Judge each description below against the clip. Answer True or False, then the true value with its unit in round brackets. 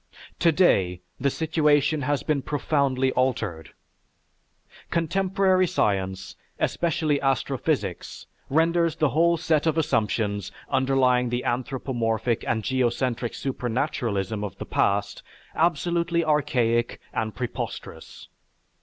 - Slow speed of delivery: True (95 wpm)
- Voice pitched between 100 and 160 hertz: True (135 Hz)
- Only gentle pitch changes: False (5.5 semitones)